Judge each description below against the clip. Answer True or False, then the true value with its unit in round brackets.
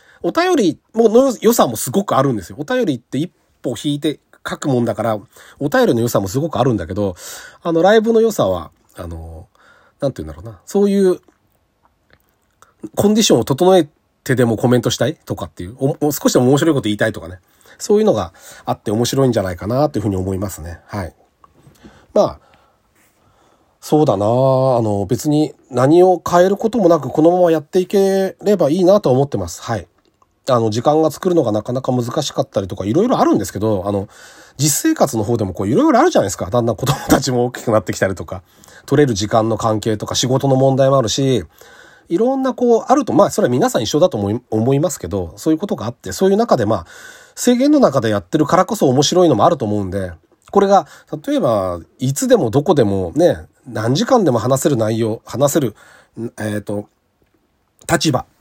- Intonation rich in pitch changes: True (8.5 semitones)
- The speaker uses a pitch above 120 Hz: True (130 Hz)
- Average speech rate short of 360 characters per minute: False (400 characters per minute)